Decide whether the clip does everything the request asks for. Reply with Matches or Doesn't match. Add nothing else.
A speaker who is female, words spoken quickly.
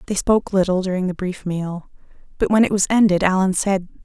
Matches